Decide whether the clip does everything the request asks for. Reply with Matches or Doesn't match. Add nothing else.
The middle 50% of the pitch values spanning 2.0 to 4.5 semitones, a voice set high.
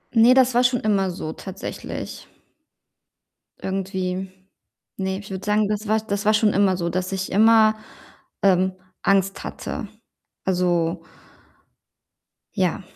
Matches